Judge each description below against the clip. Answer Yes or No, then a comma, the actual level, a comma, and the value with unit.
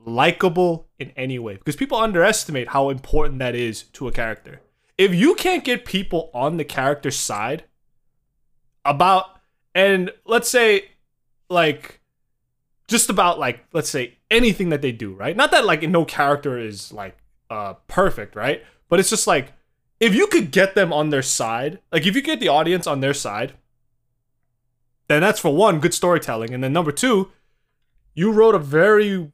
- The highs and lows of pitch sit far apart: Yes, wide, 7.0 semitones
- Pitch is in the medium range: Yes, medium, 150 Hz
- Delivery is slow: No, average, 170 wpm